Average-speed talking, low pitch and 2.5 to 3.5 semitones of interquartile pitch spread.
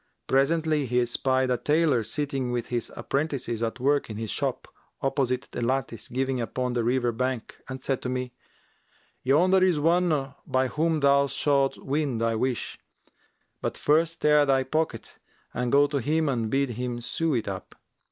Yes: average, 170 wpm; low, 130 Hz; average, 3.1 semitones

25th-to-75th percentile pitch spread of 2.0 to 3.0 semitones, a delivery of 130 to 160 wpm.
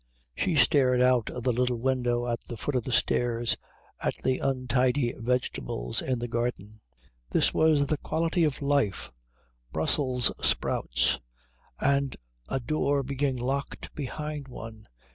Yes: average, 2.7 semitones; average, 140 wpm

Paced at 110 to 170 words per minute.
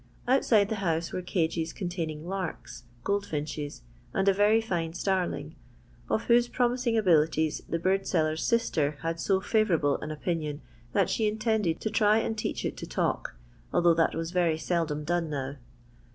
Yes: average, 165 wpm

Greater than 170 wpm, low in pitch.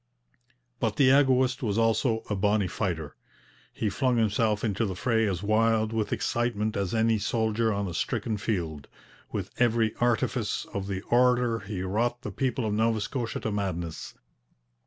No: average, 160 wpm; low, 110 Hz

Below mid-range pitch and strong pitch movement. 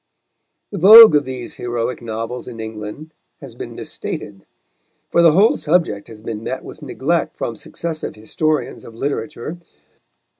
Yes: low, 130 Hz; wide, 5.9 semitones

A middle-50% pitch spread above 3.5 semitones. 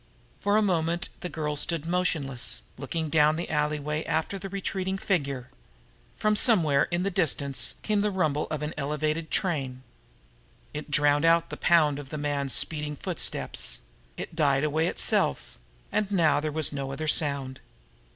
No: average, 3.2 semitones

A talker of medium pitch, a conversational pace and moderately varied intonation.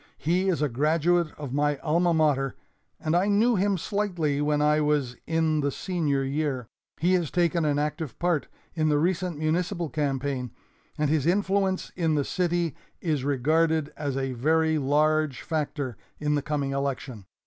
Yes: medium, 155 Hz; average, 165 wpm; average, 3.1 semitones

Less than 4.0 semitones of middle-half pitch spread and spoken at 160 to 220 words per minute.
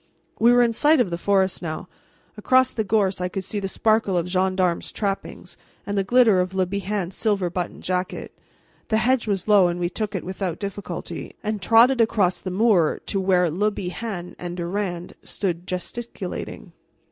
Yes: average, 3.1 semitones; average, 180 wpm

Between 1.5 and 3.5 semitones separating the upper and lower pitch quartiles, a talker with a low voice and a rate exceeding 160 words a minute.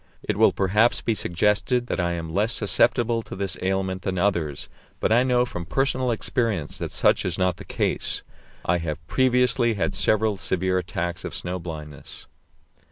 No: average, 4.8 semitones; very low, 95 Hz; average, 170 wpm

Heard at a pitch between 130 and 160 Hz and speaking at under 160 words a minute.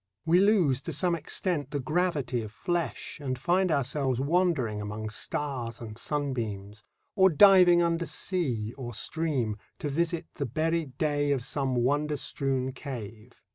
Yes: medium, 140 Hz; average, 145 wpm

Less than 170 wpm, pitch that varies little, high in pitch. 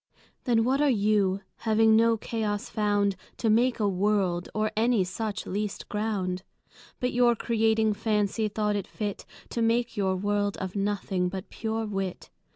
Yes: average, 160 wpm; narrow, 2.1 semitones; high, 210 Hz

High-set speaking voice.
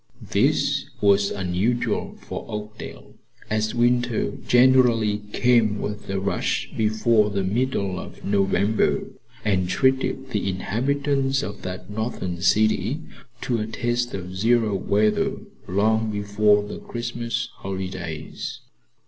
No: low, 105 Hz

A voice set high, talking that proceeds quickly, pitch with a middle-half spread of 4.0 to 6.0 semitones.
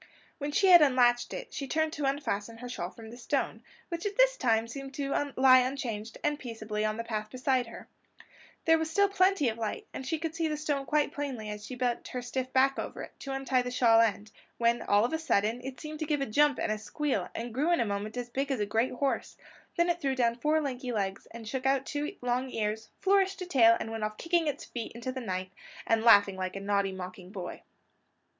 Yes: very high, 250 Hz; fast, 235 wpm; average, 4.7 semitones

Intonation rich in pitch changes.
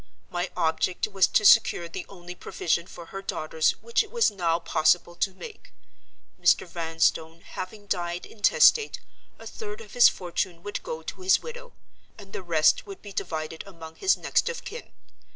No: average, 4.4 semitones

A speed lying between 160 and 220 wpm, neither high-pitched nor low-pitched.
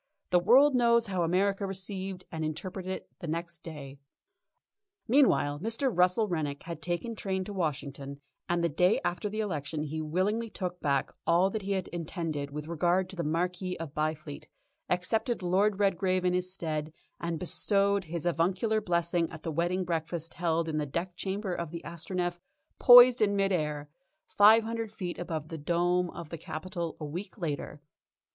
Yes: average, 175 wpm; medium, 175 Hz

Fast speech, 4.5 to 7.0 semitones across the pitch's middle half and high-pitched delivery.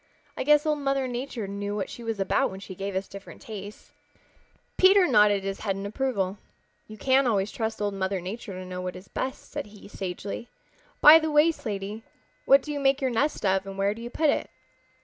Yes: fast, 215 wpm; wide, 5.5 semitones; high, 210 Hz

